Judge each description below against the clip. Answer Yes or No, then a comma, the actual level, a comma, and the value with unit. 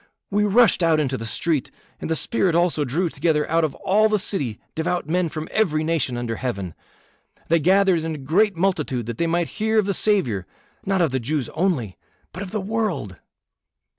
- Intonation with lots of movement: Yes, wide, 5.8 semitones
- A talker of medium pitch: Yes, medium, 165 Hz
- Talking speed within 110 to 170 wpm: No, average, 195 wpm